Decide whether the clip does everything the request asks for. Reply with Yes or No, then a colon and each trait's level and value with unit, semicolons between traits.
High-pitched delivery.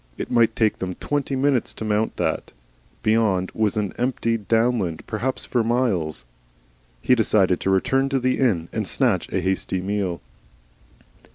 No: low, 110 Hz